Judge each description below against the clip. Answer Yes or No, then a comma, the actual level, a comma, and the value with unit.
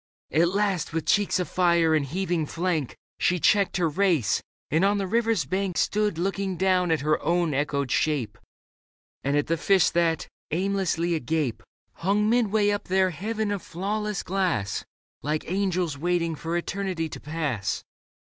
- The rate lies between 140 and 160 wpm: Yes, average, 155 wpm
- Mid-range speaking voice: Yes, medium, 175 Hz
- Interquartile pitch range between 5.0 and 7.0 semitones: No, average, 3.8 semitones